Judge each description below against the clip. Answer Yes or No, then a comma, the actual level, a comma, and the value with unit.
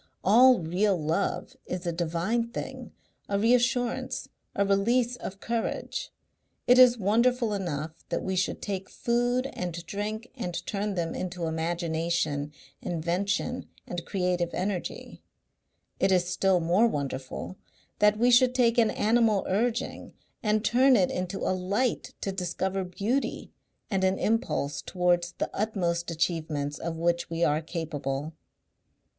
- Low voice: No, high, 190 Hz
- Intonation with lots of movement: No, average, 4.8 semitones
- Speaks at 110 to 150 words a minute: Yes, slow, 135 wpm